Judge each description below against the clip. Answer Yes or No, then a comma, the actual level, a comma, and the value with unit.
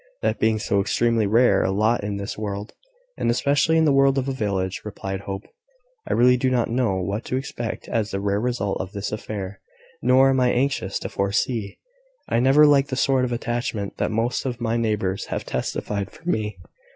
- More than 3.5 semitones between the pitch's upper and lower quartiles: Yes, average, 4.2 semitones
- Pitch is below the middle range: Yes, low, 115 Hz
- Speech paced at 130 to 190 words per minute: No, average, 200 wpm